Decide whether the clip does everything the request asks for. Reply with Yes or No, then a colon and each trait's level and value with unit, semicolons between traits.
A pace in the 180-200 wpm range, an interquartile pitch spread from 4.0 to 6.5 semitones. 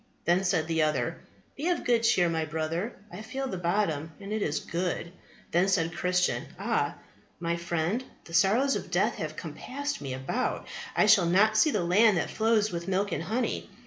Yes: average, 190 wpm; average, 4.5 semitones